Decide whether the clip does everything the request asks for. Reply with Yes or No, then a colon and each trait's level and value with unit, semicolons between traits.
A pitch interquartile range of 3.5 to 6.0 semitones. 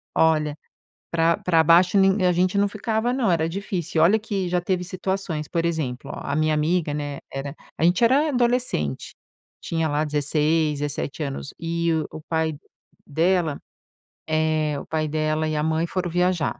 No: average, 3.1 semitones